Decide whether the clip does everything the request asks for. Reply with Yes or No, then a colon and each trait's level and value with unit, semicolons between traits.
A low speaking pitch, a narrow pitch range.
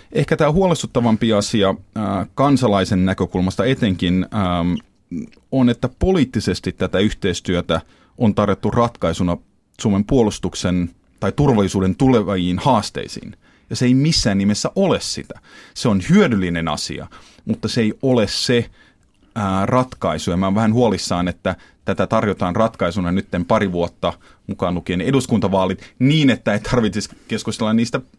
No: low, 100 Hz; average, 4.0 semitones